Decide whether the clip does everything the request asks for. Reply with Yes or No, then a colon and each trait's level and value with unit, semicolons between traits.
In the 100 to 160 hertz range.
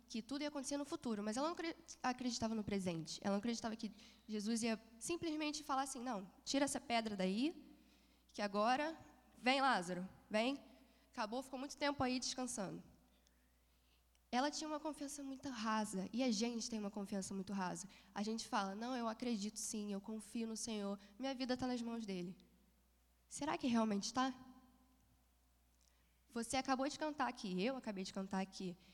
No: high, 230 Hz